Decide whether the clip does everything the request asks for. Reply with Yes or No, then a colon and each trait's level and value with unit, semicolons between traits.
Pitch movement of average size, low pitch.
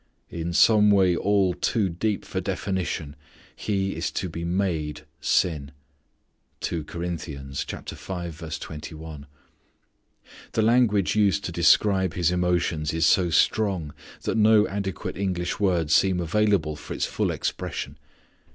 Yes: average, 3.5 semitones; very low, 90 Hz